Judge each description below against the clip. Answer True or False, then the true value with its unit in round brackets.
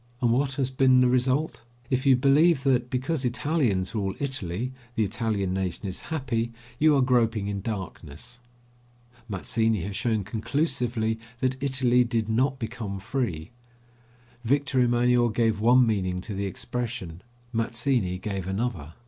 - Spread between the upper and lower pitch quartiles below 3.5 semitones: False (4.2 semitones)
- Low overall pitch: True (120 Hz)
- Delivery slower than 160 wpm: True (140 wpm)